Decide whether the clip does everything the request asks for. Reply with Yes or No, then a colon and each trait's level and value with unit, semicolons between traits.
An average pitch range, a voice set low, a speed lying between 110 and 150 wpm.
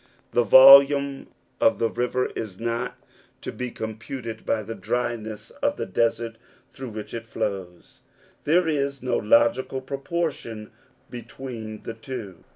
Yes: average, 3.1 semitones; low, 115 Hz; slow, 135 wpm